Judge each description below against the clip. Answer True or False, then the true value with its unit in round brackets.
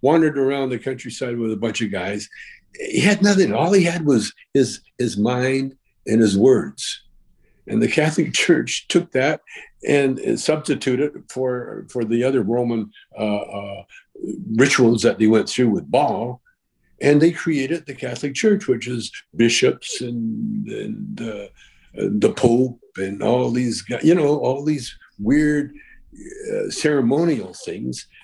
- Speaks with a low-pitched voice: True (130 Hz)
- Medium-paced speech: True (150 wpm)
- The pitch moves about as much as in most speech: False (5.8 semitones)